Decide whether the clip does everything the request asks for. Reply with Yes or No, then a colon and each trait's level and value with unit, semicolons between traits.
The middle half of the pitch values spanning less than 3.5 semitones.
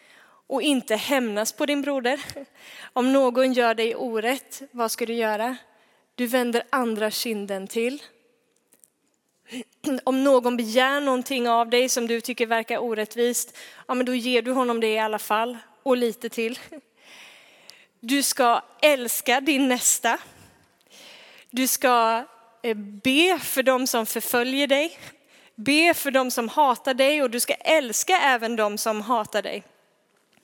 Yes: average, 2.7 semitones